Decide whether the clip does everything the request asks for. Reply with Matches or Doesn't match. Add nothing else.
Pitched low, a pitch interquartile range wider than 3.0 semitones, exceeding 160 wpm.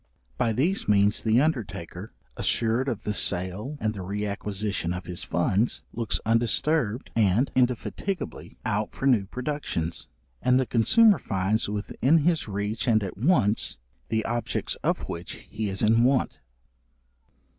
Doesn't match